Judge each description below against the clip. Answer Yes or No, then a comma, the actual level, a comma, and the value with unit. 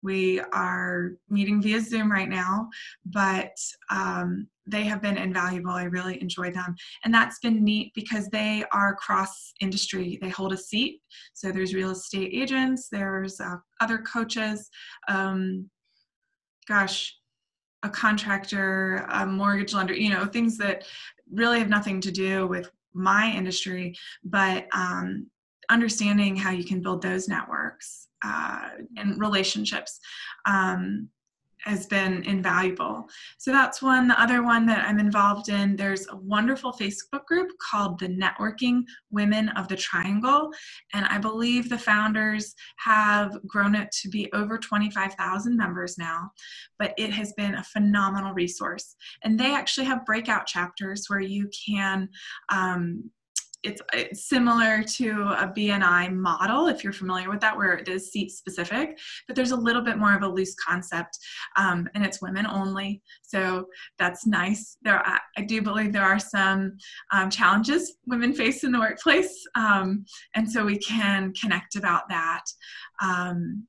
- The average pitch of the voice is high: Yes, high, 200 Hz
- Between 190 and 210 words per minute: No, average, 150 wpm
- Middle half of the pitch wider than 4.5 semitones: No, narrow, 2.6 semitones